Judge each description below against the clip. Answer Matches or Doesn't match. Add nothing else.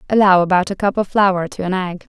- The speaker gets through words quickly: Matches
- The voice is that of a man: Doesn't match